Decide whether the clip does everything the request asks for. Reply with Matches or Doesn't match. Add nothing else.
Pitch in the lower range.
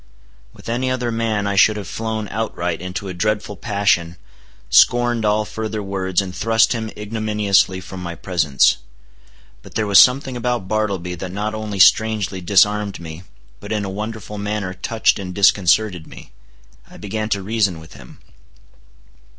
Matches